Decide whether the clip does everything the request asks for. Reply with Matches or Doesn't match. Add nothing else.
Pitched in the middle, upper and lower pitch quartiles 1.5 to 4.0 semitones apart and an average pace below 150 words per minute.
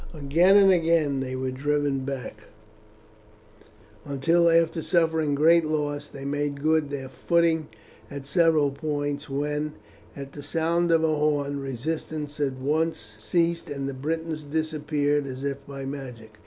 Matches